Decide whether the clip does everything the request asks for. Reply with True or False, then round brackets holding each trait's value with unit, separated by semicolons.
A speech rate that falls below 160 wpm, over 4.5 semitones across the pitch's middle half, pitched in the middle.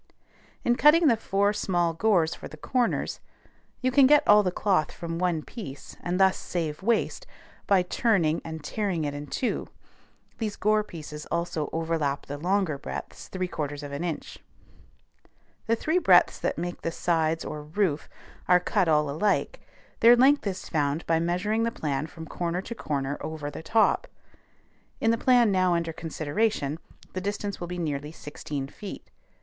False (165 wpm; 5.2 semitones; 175 Hz)